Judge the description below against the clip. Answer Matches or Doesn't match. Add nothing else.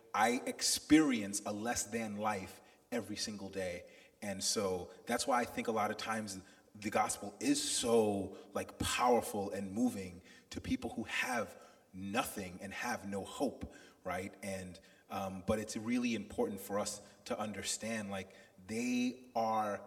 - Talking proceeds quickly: Doesn't match